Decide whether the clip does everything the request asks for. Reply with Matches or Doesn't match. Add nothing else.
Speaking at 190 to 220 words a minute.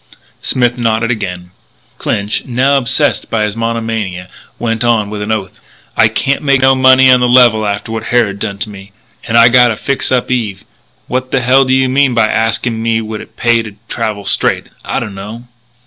Matches